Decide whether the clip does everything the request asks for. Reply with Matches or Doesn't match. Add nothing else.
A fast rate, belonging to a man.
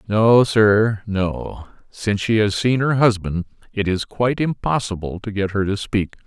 Doesn't match